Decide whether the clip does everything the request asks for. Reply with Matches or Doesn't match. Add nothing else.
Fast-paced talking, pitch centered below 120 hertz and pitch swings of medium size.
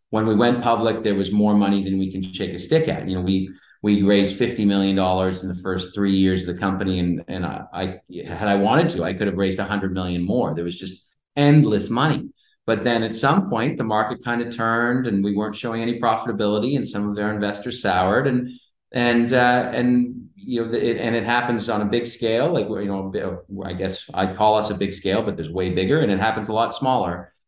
Matches